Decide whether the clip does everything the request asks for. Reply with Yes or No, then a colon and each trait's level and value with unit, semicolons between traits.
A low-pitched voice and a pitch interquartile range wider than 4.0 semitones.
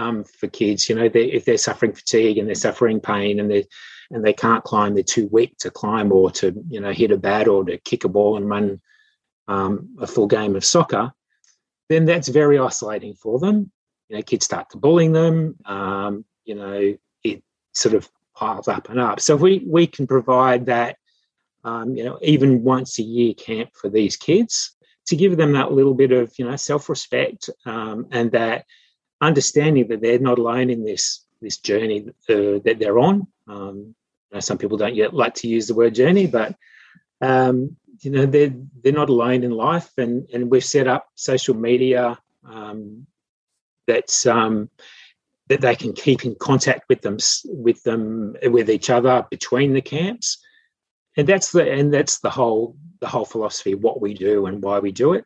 Yes: low, 120 Hz; average, 4.5 semitones